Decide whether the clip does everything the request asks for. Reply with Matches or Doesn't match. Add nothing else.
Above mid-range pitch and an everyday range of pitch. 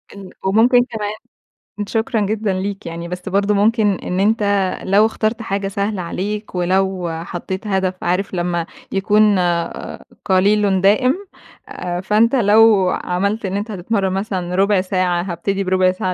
Doesn't match